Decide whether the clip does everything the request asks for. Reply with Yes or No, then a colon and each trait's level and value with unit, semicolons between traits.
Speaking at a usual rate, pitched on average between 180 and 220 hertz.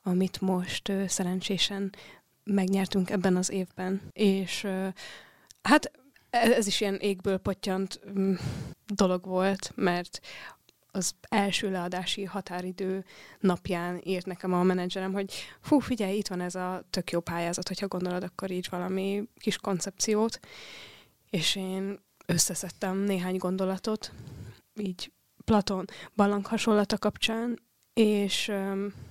Yes: average, 120 wpm; high, 190 Hz